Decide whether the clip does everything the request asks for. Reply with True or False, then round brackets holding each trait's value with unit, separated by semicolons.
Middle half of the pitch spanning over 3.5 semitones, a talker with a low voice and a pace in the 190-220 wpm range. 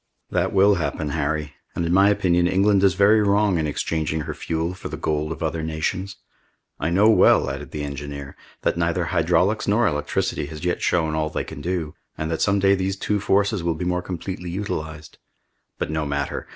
True (3.9 semitones; 85 Hz; 200 wpm)